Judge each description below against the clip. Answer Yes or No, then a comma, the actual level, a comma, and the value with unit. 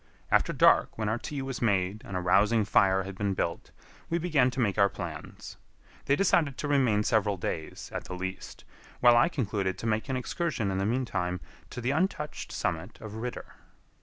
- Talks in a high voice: No, low, 110 Hz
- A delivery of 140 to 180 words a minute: No, average, 195 wpm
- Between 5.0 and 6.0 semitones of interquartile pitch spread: Yes, average, 5.3 semitones